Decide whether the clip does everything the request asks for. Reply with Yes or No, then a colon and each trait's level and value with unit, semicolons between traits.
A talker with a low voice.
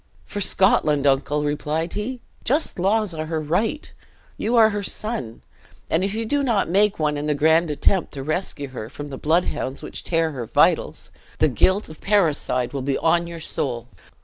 No: medium, 160 Hz